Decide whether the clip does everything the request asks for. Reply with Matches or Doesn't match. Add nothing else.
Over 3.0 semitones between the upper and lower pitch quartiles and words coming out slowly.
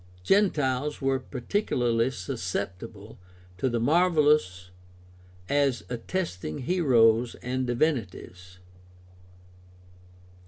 Matches